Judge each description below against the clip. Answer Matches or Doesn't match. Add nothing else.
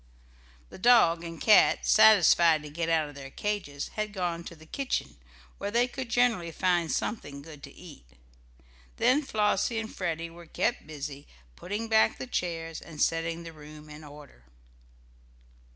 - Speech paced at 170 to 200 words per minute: Doesn't match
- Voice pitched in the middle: Matches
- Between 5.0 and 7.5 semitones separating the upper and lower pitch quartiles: Matches